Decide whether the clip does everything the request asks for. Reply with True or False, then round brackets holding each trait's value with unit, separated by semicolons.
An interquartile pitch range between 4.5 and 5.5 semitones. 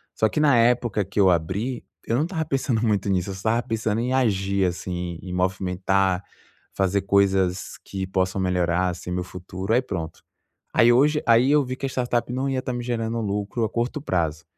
True (4.8 semitones)